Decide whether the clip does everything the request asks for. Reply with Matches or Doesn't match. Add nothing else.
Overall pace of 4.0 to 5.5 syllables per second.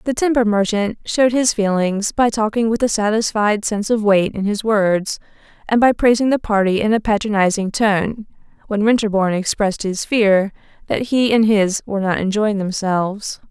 Matches